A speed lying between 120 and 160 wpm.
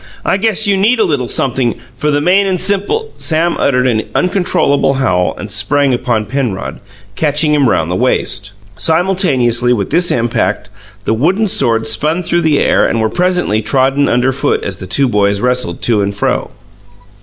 No: average, 180 wpm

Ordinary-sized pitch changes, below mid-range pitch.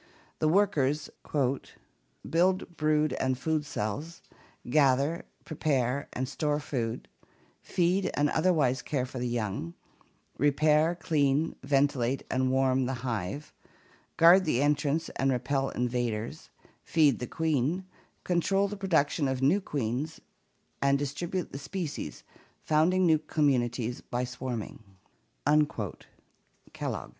No: average, 3.8 semitones; medium, 145 Hz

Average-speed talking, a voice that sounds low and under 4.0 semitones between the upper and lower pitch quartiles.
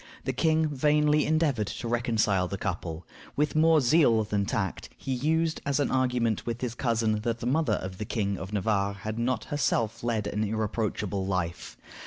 No: average, 180 wpm; low, 115 Hz; wide, 5.5 semitones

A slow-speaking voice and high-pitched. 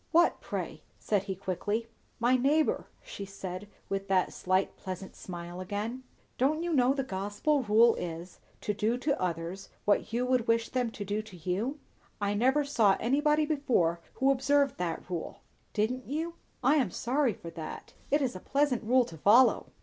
No: average, 175 wpm; high, 225 Hz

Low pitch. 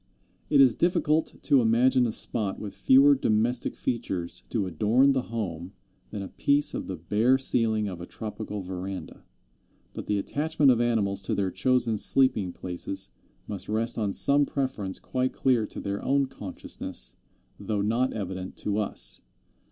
Yes: low, 110 Hz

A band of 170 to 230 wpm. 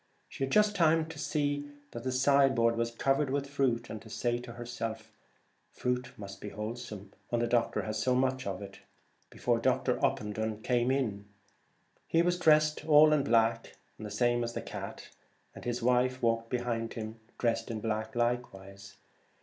Yes: average, 175 wpm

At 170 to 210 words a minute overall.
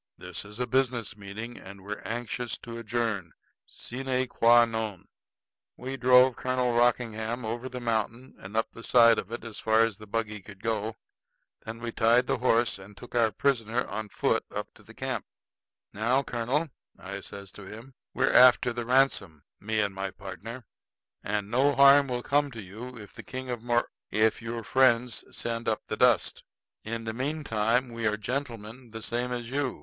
Yes: average, 185 wpm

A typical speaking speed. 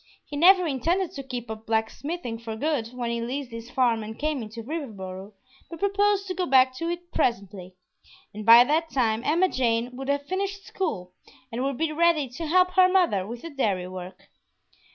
Yes: average, 195 wpm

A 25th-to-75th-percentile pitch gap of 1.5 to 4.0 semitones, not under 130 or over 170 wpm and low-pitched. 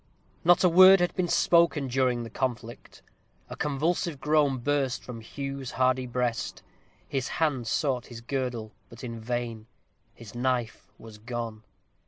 Yes: average, 3.5 semitones; average, 145 wpm; low, 130 Hz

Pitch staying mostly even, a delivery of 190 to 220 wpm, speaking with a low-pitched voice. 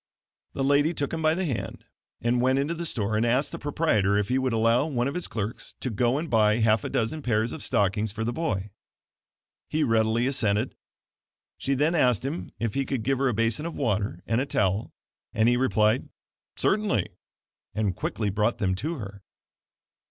No: average, 4.5 semitones; average, 195 wpm; low, 120 Hz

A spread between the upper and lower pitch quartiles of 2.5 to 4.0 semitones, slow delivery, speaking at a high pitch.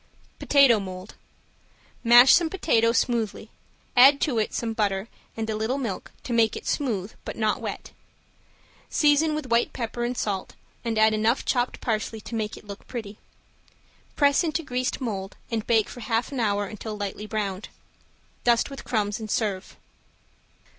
No: average, 2.8 semitones; average, 160 wpm; high, 225 Hz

